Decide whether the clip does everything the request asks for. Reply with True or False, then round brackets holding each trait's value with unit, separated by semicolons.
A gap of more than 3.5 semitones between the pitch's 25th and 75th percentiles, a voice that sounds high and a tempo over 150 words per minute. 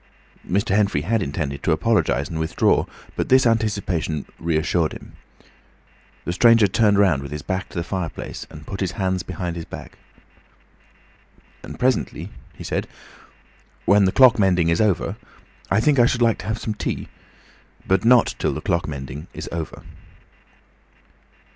False (5.0 semitones; 95 Hz; 160 wpm)